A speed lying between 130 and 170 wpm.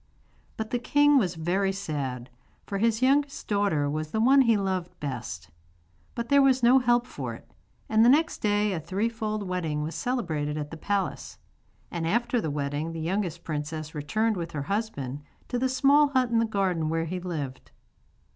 No: average, 185 wpm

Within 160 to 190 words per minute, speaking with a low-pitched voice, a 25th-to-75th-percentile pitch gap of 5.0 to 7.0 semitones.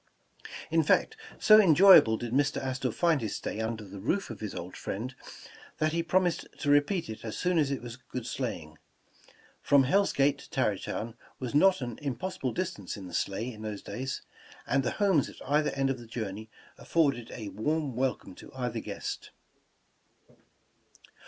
Yes: average, 180 wpm; low, 130 Hz; wide, 5.6 semitones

